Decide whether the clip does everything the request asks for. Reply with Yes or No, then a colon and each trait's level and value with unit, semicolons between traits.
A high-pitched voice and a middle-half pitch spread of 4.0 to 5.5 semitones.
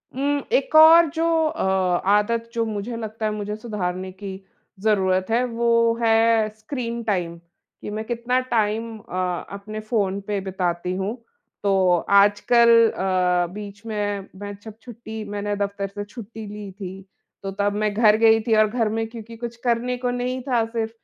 No: high, 215 Hz; narrow, 2.6 semitones